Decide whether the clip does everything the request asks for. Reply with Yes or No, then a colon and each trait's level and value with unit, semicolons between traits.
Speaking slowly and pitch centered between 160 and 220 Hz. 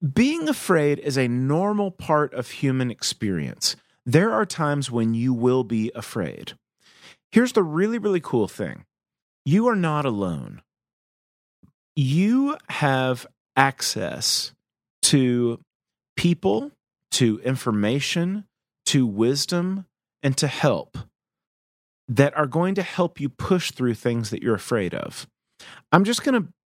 No: slow, 125 wpm; medium, 145 Hz